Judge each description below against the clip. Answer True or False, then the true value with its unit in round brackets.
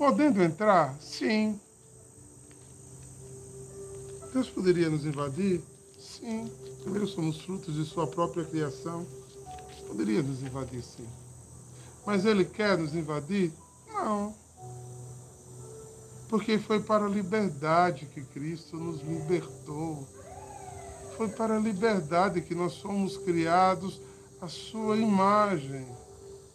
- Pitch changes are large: True (7.2 semitones)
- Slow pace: True (105 wpm)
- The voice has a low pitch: False (165 Hz)